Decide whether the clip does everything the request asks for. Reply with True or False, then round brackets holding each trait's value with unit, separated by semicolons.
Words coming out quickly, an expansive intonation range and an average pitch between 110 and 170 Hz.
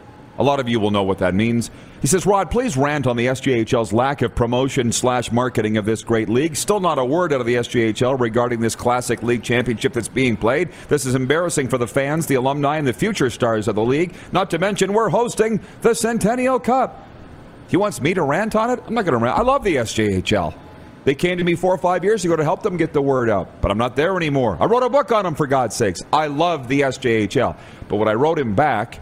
True (250 wpm; 7.3 semitones; 135 Hz)